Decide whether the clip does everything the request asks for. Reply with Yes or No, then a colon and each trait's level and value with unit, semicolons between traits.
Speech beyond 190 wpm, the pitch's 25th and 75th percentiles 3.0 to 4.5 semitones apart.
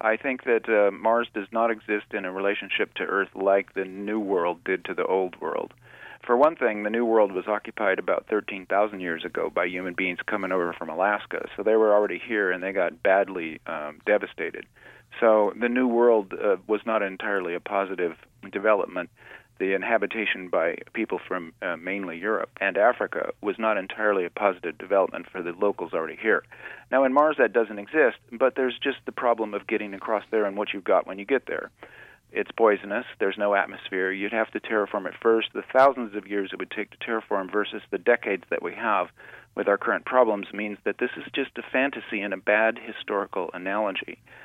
No: average, 200 wpm; narrow, 2.4 semitones